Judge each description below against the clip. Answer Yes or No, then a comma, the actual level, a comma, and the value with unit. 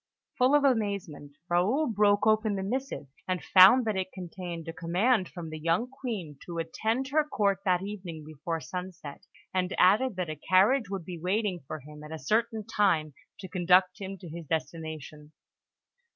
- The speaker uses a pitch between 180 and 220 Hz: Yes, medium, 185 Hz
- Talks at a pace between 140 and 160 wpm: No, average, 175 wpm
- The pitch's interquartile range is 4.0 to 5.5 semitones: Yes, average, 4.4 semitones